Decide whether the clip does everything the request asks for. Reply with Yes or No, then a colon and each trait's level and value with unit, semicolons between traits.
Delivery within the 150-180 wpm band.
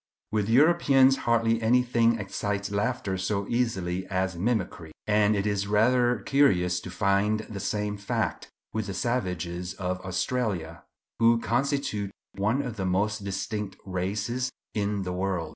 No: average, 140 wpm